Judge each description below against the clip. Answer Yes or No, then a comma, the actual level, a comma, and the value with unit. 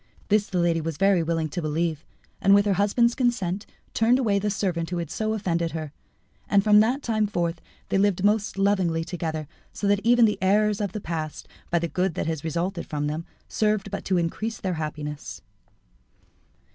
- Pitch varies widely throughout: No, average, 4.0 semitones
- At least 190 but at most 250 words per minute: Yes, average, 195 wpm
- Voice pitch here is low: No, high, 190 Hz